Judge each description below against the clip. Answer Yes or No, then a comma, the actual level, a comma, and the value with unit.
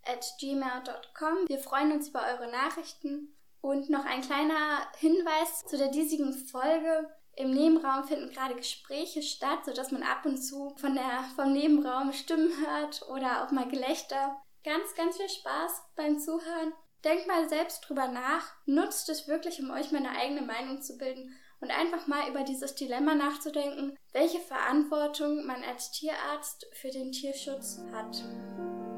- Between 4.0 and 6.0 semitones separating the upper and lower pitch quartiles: No, average, 2.9 semitones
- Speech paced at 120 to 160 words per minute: Yes, average, 155 wpm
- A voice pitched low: No, very high, 285 Hz